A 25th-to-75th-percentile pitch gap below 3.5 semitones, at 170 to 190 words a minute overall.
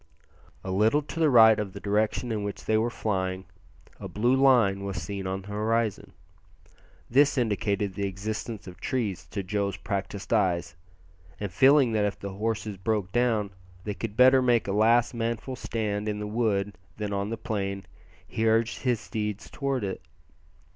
Yes: average, 2.7 semitones; average, 175 wpm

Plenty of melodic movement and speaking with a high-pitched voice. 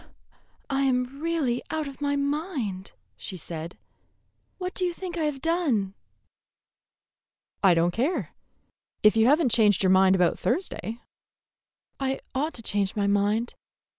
Yes: wide, 7.1 semitones; very high, 250 Hz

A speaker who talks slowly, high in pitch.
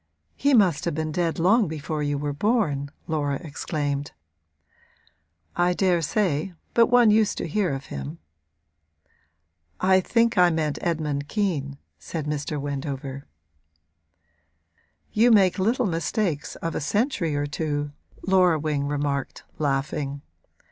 No: slow, 125 wpm; medium, 155 Hz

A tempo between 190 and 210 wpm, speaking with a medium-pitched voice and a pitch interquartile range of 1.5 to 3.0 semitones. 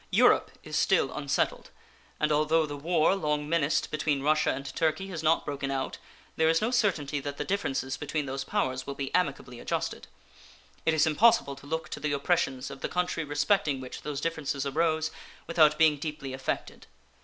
No: average, 180 wpm; medium, 150 Hz; average, 2.7 semitones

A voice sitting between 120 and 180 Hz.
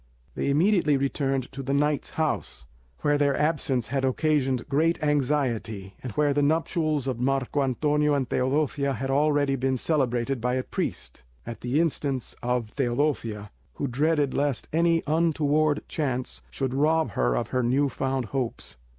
Yes: medium, 140 Hz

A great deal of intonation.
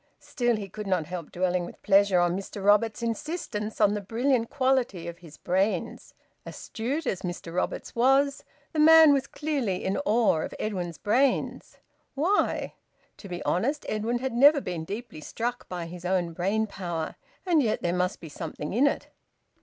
Yes: wide, 6.2 semitones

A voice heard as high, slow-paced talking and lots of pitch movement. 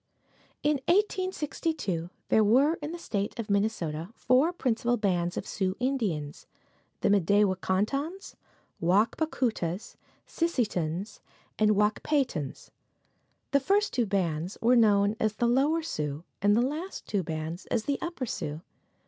No: high, 215 Hz; average, 155 wpm; wide, 7.0 semitones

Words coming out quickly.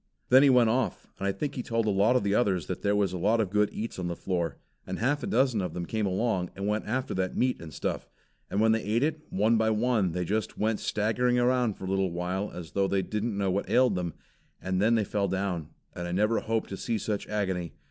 Yes: fast, 260 wpm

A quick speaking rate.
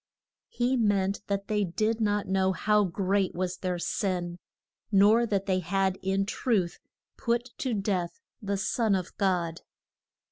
No: average, 145 wpm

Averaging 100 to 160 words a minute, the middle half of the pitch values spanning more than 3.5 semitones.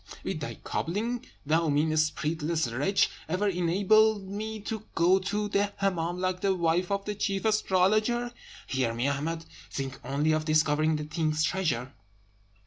Yes: average, 150 wpm; average, 4.5 semitones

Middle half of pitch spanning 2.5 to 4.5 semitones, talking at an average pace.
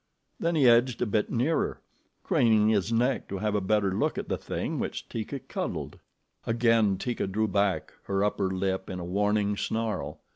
Yes: average, 2.9 semitones; average, 180 wpm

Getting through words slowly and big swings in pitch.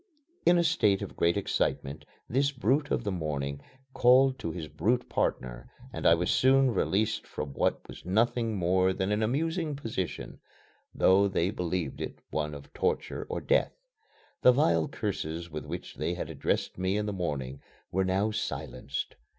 No: average, 165 wpm; wide, 6.9 semitones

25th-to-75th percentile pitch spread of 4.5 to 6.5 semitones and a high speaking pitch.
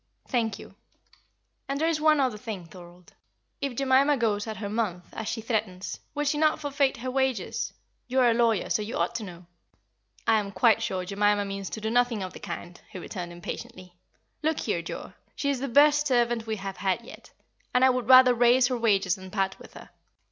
Yes: average, 4.8 semitones; high, 225 Hz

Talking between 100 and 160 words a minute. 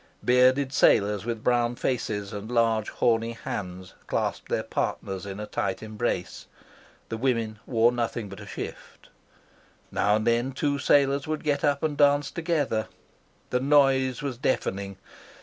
Yes: average, 150 wpm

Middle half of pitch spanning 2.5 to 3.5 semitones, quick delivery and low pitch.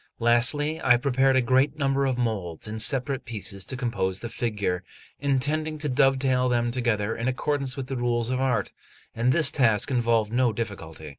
No: average, 2.9 semitones; average, 175 wpm; low, 125 Hz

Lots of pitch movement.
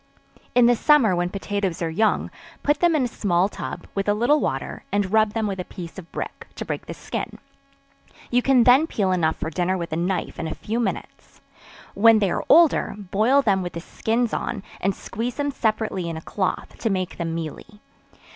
No: average, 4.8 semitones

